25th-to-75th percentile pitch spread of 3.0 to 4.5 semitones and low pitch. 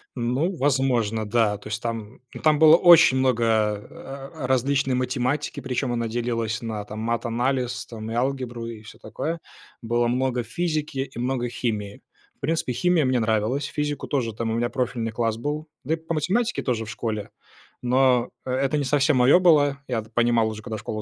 Yes: average, 3.4 semitones; low, 125 Hz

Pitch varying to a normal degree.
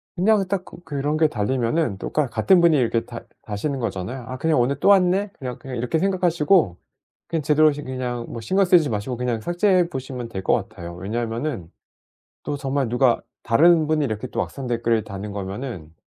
No: wide, 5.7 semitones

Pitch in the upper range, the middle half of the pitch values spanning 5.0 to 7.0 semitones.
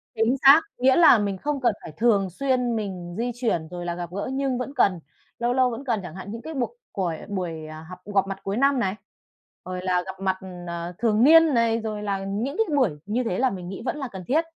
Yes: high, 215 Hz; wide, 5.5 semitones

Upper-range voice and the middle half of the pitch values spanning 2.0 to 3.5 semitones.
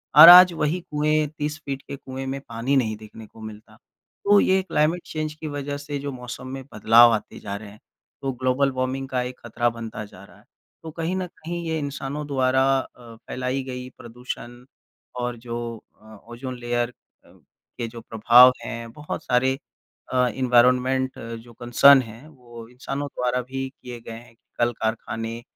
No: low, 130 Hz; average, 3.1 semitones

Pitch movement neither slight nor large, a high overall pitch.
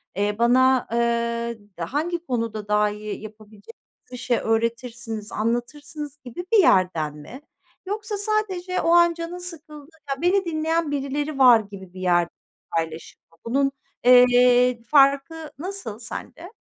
No: wide, 6.3 semitones; very high, 250 Hz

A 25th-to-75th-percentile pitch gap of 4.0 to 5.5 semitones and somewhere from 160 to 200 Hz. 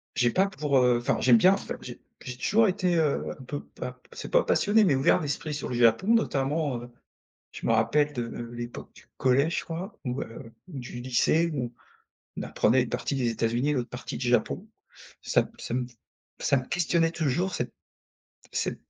No: average, 5.2 semitones; low, 135 Hz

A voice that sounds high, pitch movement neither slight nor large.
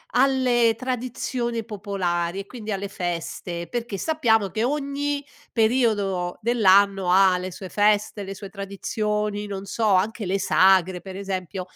Yes: high, 205 Hz; average, 3.6 semitones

